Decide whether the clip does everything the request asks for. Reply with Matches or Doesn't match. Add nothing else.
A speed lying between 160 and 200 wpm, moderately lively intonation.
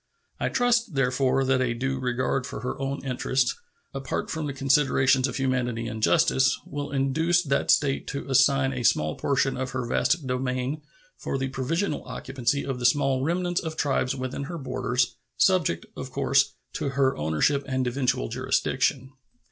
Doesn't match